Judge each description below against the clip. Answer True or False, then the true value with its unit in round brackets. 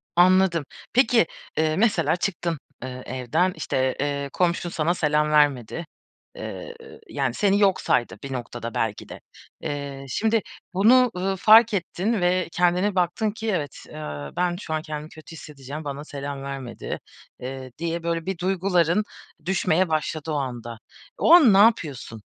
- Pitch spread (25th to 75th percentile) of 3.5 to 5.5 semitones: True (5.2 semitones)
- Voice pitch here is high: False (165 Hz)